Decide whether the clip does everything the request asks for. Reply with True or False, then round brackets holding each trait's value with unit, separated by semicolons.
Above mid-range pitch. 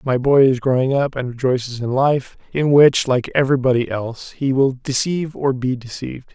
False (130 Hz)